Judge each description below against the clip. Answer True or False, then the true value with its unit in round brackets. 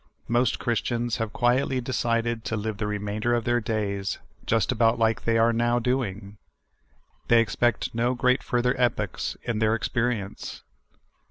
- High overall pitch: False (115 Hz)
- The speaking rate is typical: True (155 wpm)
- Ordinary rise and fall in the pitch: False (2.0 semitones)